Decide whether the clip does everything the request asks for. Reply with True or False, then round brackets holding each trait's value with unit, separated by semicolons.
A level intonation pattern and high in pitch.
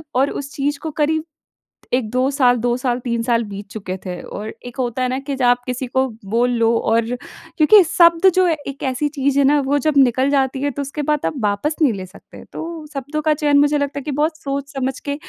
False (3.0 semitones; 270 Hz)